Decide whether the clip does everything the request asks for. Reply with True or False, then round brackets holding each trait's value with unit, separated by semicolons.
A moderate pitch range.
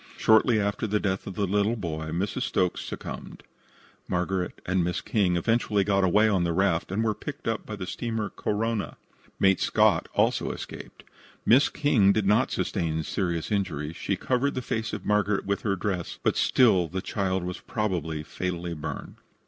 True (3.4 semitones)